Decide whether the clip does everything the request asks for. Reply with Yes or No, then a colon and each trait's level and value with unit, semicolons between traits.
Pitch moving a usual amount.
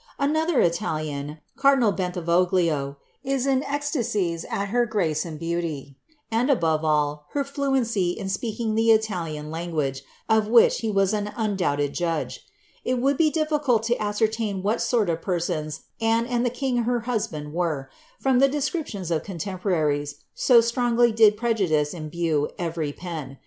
No: wide, 6.8 semitones